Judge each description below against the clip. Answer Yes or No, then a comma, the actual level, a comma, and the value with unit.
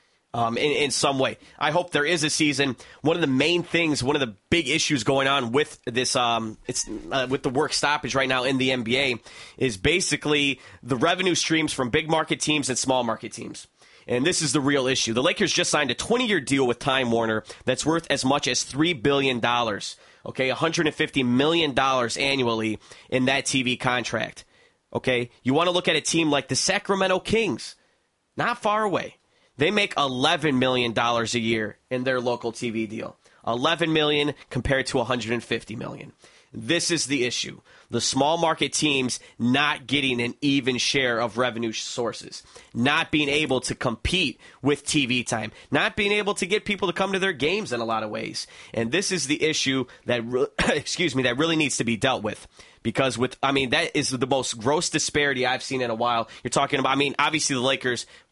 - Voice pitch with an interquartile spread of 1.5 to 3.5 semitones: No, average, 4.0 semitones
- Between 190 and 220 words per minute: Yes, average, 200 wpm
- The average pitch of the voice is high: No, low, 135 Hz